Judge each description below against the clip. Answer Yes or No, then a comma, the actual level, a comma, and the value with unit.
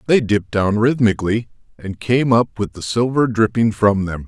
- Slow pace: No, average, 180 wpm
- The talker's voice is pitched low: Yes, low, 110 Hz